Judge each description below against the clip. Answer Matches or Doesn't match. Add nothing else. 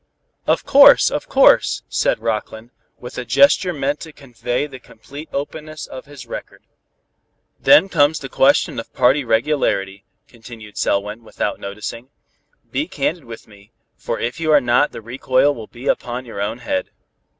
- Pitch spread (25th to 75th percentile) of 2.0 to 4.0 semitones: Doesn't match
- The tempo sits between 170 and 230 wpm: Doesn't match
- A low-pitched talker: Matches